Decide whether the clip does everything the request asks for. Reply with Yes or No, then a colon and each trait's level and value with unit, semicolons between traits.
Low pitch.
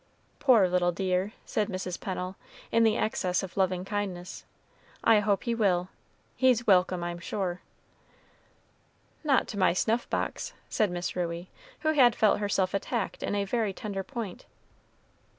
No: high, 195 Hz